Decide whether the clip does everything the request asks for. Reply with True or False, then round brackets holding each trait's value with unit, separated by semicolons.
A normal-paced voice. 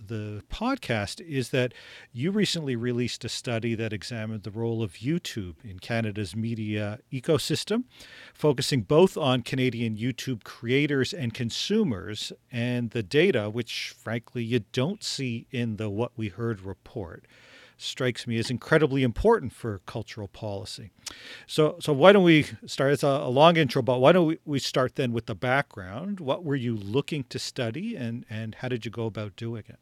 True (170 wpm)